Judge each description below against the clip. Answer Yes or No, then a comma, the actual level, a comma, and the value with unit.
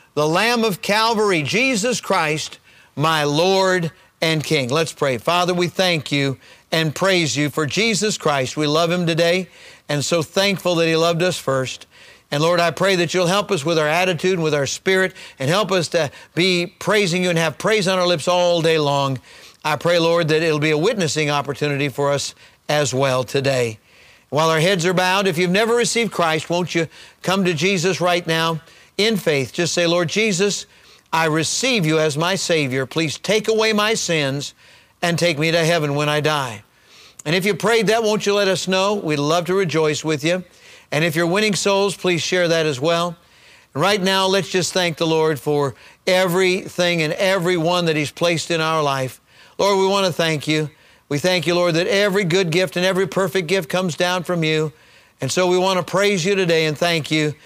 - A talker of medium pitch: Yes, medium, 170 Hz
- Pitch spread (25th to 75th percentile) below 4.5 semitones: Yes, average, 3.4 semitones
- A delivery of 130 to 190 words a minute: No, fast, 205 wpm